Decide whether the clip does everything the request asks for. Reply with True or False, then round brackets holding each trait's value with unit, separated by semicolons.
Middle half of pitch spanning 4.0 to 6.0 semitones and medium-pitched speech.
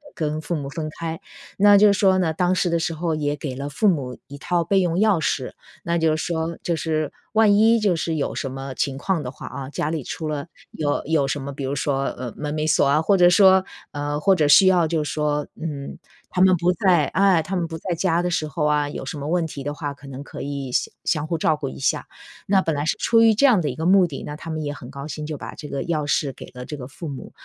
False (3.5 semitones; 155 Hz)